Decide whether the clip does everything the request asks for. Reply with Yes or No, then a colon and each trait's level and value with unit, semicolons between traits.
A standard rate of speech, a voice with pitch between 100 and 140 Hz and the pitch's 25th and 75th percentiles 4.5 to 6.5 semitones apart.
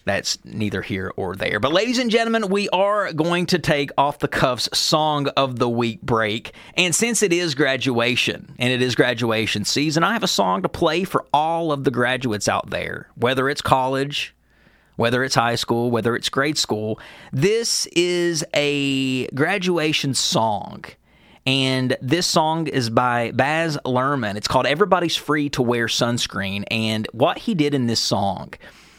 Yes: average, 170 wpm; low, 135 Hz; wide, 5.4 semitones